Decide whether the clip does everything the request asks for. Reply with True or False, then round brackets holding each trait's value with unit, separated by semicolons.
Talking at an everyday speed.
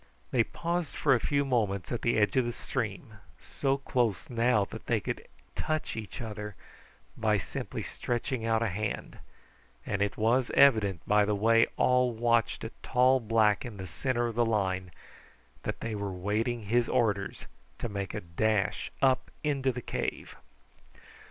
True (165 wpm)